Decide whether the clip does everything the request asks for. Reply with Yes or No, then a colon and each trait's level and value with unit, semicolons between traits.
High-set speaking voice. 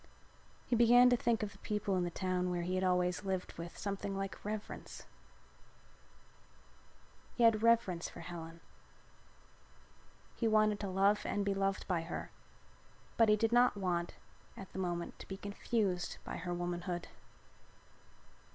Yes: high, 195 Hz